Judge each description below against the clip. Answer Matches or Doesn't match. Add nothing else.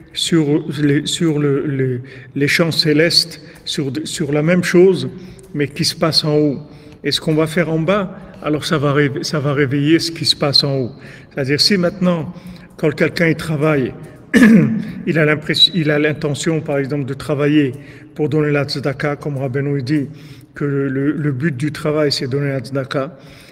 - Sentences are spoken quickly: Doesn't match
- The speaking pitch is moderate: Matches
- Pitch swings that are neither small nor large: Doesn't match